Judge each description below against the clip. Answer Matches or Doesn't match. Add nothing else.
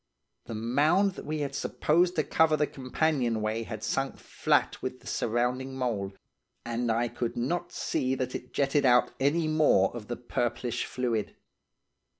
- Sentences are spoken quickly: Doesn't match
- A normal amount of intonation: Matches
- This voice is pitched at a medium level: Doesn't match